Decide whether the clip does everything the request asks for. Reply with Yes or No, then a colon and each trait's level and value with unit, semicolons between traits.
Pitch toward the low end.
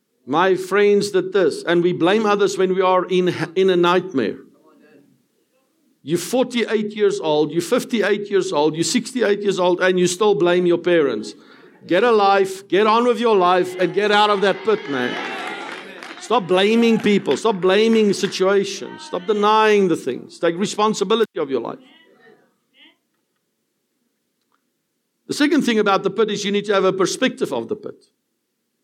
No: high, 200 Hz